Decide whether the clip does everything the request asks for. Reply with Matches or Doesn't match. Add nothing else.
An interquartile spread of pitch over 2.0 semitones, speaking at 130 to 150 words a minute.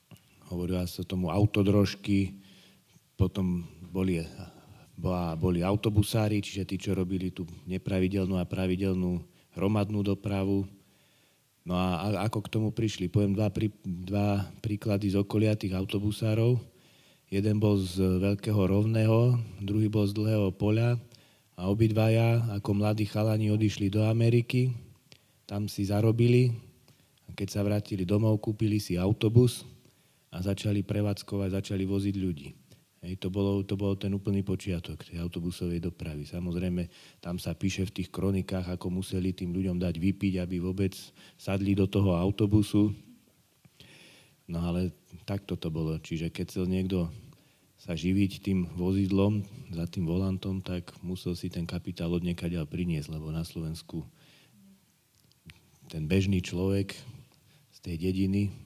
Matches